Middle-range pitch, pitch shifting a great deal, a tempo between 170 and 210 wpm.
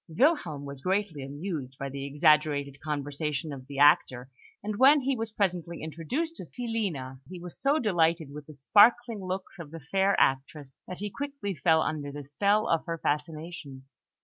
Yes: medium, 160 Hz; wide, 6.0 semitones; average, 175 wpm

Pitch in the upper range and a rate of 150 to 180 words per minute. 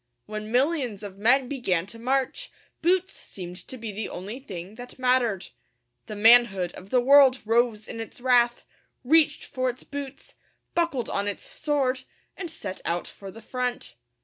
Yes: high, 245 Hz; average, 165 wpm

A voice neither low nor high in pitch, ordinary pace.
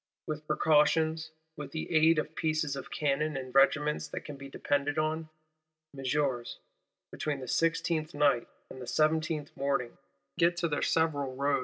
Yes: medium, 150 Hz; average, 155 wpm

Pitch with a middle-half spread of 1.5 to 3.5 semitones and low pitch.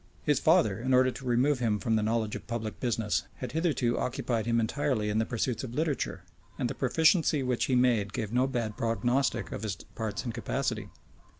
Yes: average, 3.0 semitones; low, 120 Hz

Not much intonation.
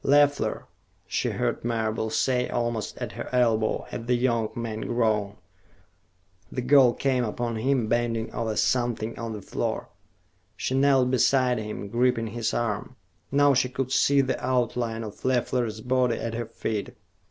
Yes: narrow, 2.3 semitones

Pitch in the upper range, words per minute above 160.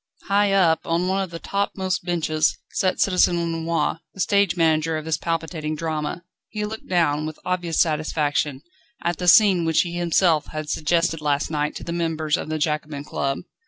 No: medium, 165 Hz; average, 180 wpm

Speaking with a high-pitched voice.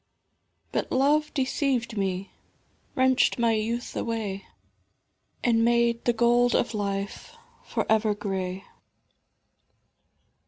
Yes: high, 230 Hz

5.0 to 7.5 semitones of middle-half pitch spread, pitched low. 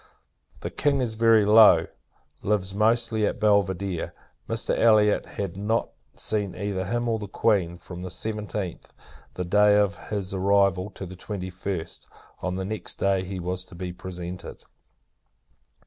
No: narrow, 2.4 semitones; low, 100 Hz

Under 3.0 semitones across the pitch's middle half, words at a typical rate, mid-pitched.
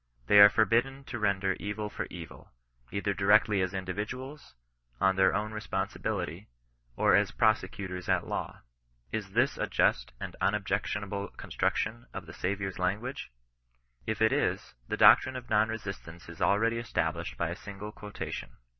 No: narrow, 2.4 semitones; average, 155 wpm; low, 100 Hz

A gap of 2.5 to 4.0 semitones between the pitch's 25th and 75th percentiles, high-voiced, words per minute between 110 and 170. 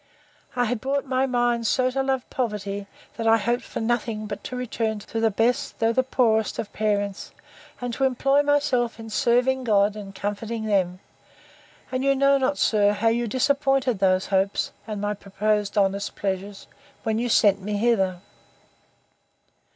Yes: average, 3.6 semitones; high, 225 Hz; average, 165 wpm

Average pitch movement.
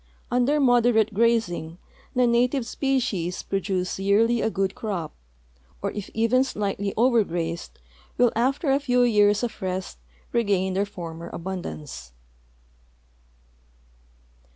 Yes: average, 4.5 semitones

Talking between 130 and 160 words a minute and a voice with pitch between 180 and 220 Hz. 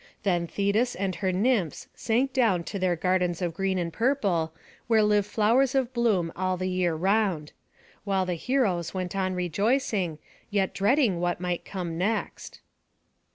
Yes: average, 155 wpm; high, 190 Hz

